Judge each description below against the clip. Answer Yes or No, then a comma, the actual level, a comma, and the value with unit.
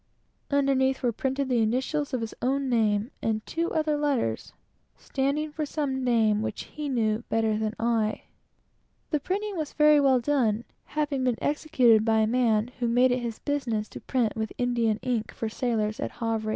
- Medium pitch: No, high, 245 Hz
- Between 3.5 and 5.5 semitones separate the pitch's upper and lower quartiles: Yes, average, 4.2 semitones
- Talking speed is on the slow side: No, average, 180 wpm